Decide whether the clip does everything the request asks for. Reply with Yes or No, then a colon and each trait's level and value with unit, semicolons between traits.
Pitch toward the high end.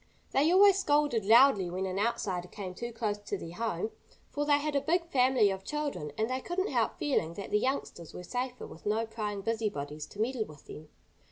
Yes: high, 225 Hz